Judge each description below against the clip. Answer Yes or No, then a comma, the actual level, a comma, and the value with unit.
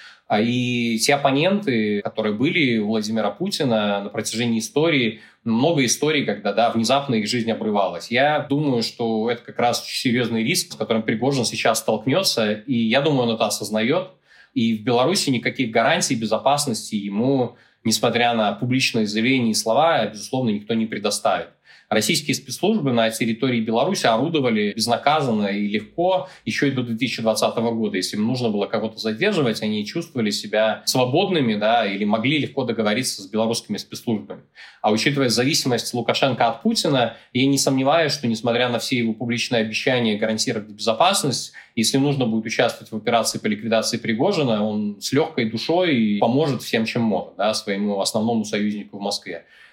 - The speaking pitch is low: Yes, low, 115 Hz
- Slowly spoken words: No, average, 155 wpm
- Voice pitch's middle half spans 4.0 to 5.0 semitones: No, average, 3.2 semitones